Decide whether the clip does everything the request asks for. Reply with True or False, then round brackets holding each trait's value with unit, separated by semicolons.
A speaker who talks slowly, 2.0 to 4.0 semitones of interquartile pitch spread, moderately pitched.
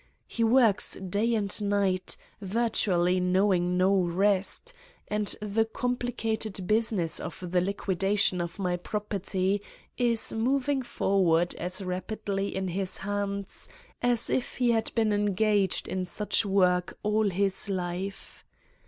False (130 wpm; 2.9 semitones; 200 Hz)